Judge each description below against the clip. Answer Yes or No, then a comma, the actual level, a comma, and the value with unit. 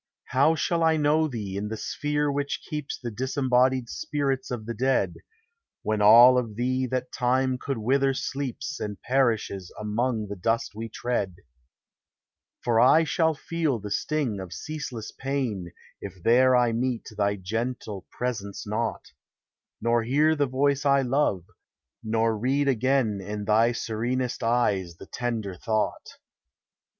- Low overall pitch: Yes, low, 125 Hz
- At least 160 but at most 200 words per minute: No, average, 145 wpm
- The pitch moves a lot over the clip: No, average, 4.0 semitones